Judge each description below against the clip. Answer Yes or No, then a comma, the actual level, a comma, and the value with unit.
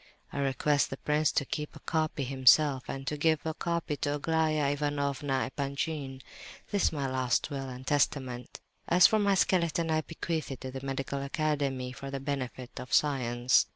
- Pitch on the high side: No, medium, 140 Hz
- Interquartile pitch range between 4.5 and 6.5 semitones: No, narrow, 2.6 semitones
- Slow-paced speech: No, average, 180 wpm